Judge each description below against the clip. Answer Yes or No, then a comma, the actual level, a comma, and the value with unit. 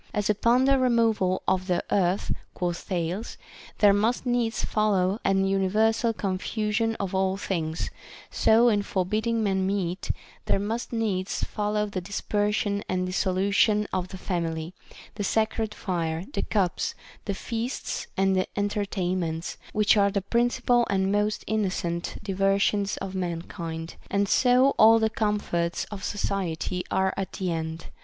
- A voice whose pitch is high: Yes, high, 200 Hz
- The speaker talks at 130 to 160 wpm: Yes, average, 145 wpm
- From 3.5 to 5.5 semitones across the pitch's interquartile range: No, average, 2.7 semitones